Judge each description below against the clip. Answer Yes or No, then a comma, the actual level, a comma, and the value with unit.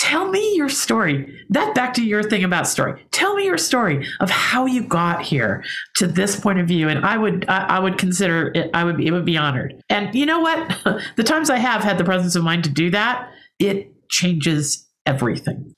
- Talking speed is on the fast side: Yes, fast, 220 wpm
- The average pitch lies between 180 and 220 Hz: Yes, high, 190 Hz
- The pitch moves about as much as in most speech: No, wide, 6.7 semitones